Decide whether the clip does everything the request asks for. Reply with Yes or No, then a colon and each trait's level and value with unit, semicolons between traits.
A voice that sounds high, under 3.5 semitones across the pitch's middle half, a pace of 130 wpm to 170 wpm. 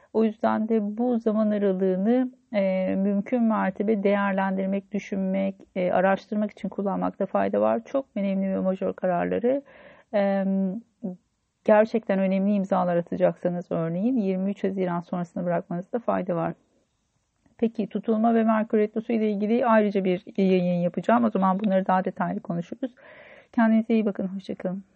Yes: high, 200 Hz; average, 2.8 semitones; average, 135 wpm